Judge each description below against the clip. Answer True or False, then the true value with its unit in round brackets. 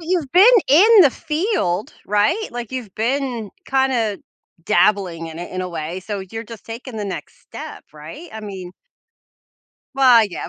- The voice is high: True (225 Hz)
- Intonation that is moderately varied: False (6.0 semitones)